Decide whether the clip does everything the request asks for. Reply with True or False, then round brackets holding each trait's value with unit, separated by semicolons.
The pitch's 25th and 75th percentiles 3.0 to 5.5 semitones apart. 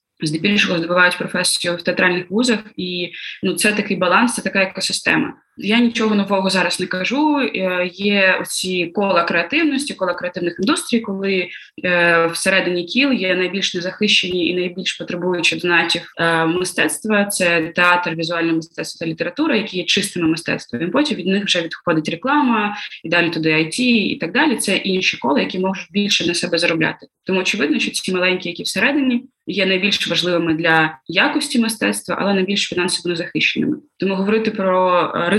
True (3.3 semitones)